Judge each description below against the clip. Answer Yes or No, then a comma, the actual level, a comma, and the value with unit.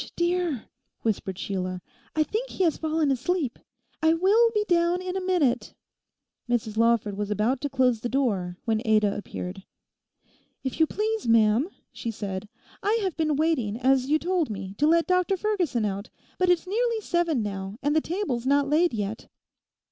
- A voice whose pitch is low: No, very high, 280 Hz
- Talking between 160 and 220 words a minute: Yes, average, 175 wpm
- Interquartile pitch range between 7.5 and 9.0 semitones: Yes, wide, 8.3 semitones